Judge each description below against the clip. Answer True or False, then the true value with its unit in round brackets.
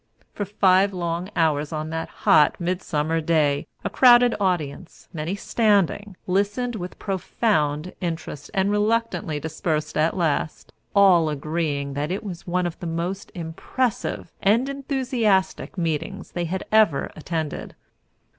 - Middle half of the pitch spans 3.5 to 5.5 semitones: True (4.3 semitones)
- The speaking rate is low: True (130 wpm)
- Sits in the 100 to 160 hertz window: False (175 Hz)